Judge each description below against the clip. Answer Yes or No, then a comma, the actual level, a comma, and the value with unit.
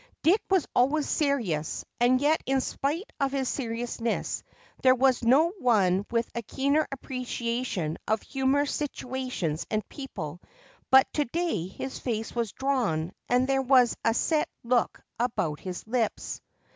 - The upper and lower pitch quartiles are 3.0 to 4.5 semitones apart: Yes, average, 3.5 semitones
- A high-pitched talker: Yes, very high, 250 Hz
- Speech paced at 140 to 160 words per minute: Yes, average, 145 wpm